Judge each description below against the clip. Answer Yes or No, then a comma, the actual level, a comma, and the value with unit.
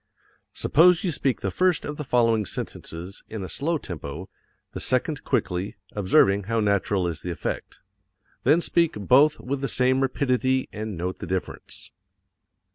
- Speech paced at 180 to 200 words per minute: No, average, 155 wpm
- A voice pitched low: Yes, low, 115 Hz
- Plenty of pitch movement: Yes, wide, 6.7 semitones